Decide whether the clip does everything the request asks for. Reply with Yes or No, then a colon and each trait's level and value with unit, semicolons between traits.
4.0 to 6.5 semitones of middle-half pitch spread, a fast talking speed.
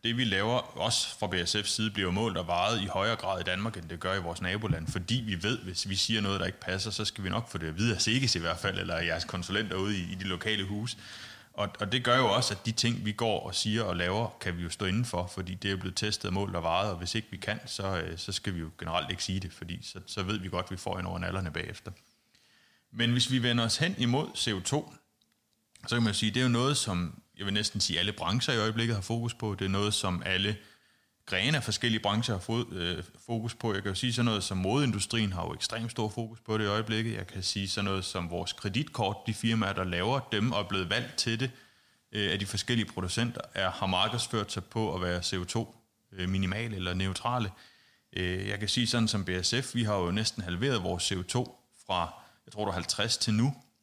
No: average, 3.5 semitones; fast, 250 wpm